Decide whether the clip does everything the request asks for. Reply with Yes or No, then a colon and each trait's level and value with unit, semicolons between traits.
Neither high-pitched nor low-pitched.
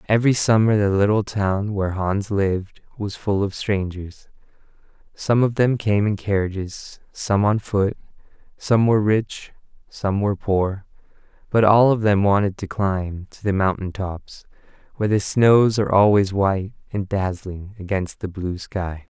No: low, 100 Hz